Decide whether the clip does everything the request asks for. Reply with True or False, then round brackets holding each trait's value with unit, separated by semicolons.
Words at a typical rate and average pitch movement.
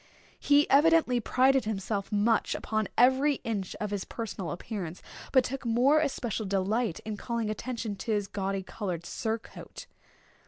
True (145 wpm; 4.1 semitones)